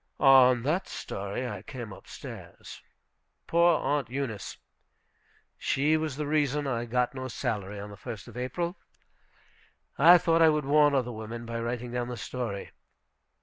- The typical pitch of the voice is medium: No, low, 125 Hz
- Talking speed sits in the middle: Yes, average, 155 wpm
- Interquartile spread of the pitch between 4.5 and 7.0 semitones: No, average, 4.0 semitones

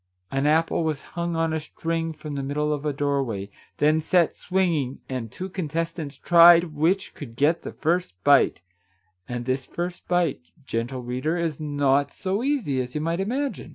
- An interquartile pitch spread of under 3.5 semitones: No, average, 3.9 semitones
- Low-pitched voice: No, medium, 150 Hz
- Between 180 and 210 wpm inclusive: Yes, average, 185 wpm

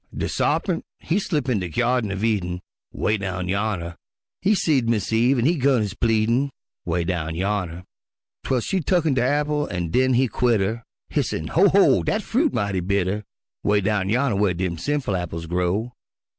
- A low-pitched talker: Yes, low, 110 Hz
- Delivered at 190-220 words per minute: No, average, 180 wpm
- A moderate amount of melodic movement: No, wide, 6.0 semitones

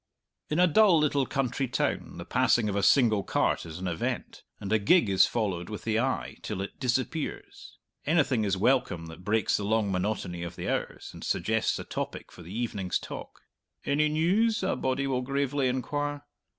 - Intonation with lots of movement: Yes, wide, 6.2 semitones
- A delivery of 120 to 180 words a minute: No, average, 190 wpm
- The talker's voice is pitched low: Yes, low, 120 Hz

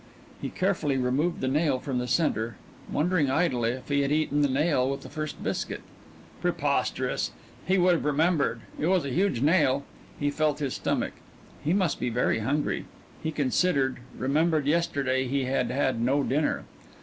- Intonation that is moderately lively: Yes, average, 3.5 semitones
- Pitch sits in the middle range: Yes, medium, 145 Hz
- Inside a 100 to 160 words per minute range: No, average, 170 wpm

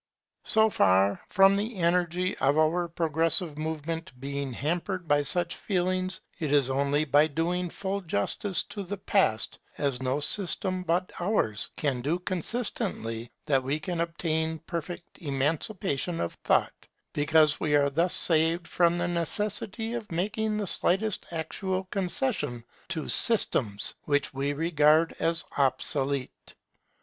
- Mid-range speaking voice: Yes, medium, 165 Hz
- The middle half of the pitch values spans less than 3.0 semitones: No, average, 4.2 semitones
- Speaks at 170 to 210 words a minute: No, slow, 135 wpm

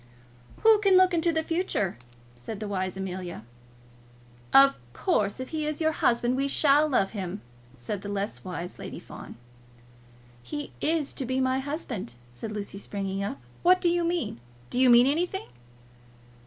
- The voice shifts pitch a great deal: Yes, wide, 8.3 semitones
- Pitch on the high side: Yes, very high, 255 Hz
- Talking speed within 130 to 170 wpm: Yes, average, 165 wpm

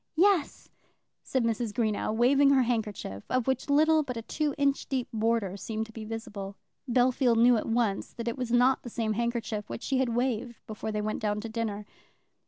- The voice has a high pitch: Yes, high, 235 Hz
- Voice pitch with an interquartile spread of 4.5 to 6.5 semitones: No, average, 2.8 semitones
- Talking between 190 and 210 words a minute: Yes, average, 195 wpm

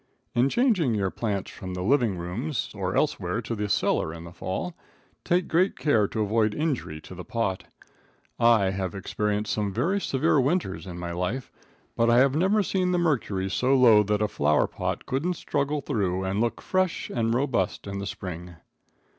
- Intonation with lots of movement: Yes, wide, 6.8 semitones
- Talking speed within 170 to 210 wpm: Yes, average, 180 wpm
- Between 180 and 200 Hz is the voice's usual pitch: No, low, 110 Hz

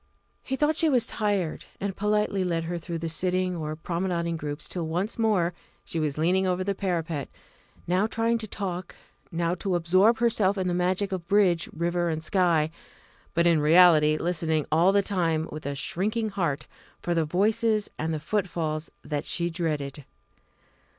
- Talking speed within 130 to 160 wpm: No, average, 170 wpm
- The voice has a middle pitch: Yes, medium, 175 Hz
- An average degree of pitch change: Yes, average, 3.3 semitones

